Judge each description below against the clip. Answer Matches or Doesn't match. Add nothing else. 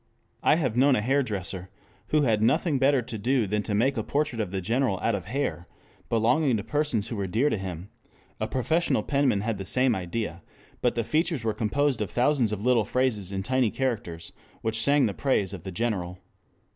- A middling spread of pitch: Matches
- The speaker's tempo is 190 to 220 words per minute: Matches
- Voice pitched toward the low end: Matches